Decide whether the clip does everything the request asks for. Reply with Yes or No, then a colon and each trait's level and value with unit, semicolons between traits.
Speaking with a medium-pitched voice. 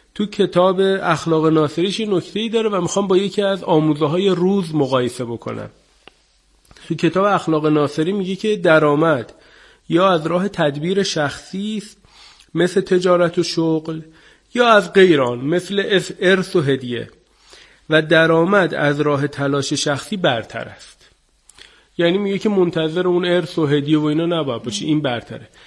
Yes: medium, 170 Hz